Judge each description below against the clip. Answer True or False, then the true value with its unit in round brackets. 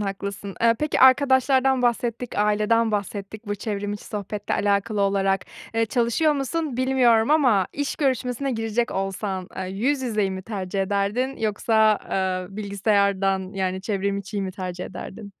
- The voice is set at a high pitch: True (210 Hz)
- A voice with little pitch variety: False (3.6 semitones)